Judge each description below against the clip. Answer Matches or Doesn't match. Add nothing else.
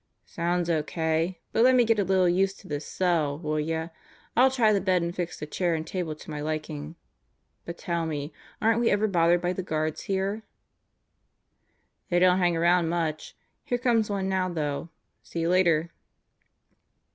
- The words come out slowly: Doesn't match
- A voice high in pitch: Doesn't match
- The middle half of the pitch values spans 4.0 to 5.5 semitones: Doesn't match